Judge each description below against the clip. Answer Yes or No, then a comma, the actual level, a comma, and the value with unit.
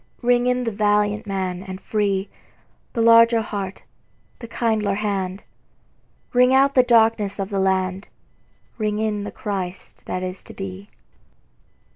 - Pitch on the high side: Yes, high, 205 Hz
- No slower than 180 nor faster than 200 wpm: No, average, 140 wpm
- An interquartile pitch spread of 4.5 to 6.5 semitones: No, average, 3.0 semitones